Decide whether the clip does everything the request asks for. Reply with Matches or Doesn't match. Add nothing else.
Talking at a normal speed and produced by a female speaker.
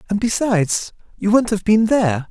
Doesn't match